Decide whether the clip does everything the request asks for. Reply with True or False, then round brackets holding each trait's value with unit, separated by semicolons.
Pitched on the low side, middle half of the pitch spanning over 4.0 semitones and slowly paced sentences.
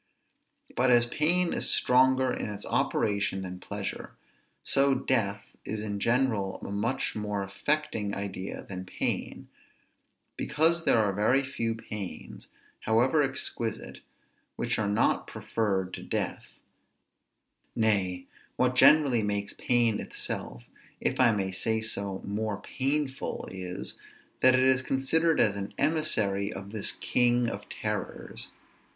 True (110 Hz; 4.5 semitones; 130 wpm)